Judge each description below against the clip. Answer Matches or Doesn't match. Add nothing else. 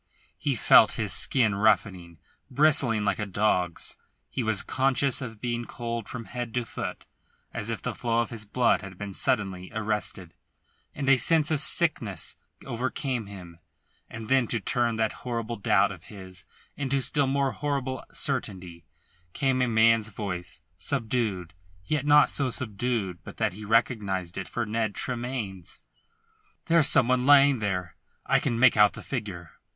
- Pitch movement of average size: Matches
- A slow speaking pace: Doesn't match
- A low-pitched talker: Matches